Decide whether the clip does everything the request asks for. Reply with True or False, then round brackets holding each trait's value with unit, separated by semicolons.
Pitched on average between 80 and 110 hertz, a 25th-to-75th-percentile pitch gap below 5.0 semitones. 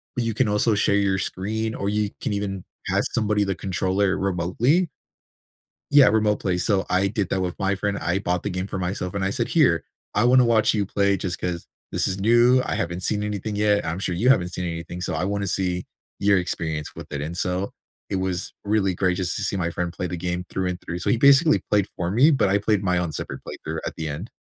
True (95 Hz; 2.7 semitones)